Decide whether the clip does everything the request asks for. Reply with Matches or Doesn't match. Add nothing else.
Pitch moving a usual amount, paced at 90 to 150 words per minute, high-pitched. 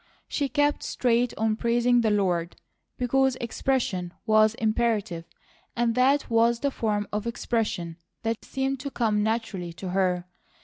Matches